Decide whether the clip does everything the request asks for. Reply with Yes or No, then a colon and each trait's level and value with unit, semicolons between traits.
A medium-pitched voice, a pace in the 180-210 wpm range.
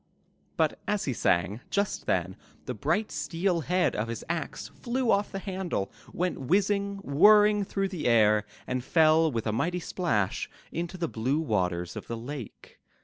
No: medium, 160 Hz; average, 170 wpm